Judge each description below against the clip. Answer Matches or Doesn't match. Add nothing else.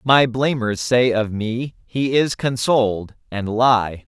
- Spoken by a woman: Doesn't match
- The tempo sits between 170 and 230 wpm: Doesn't match